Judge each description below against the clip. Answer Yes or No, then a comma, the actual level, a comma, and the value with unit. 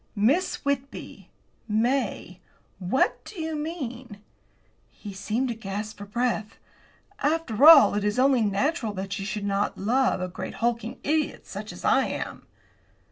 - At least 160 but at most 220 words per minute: No, average, 145 wpm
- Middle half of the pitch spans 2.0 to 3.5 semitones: No, wide, 5.4 semitones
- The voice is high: Yes, high, 235 Hz